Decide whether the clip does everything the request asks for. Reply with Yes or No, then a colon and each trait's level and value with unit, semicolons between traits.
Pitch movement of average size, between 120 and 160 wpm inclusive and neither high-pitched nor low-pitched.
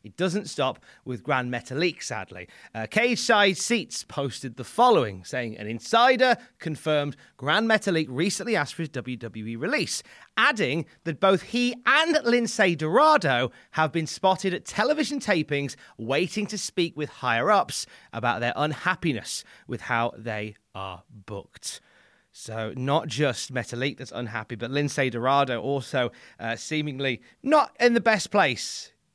No: wide, 8.1 semitones; average, 145 wpm; medium, 145 Hz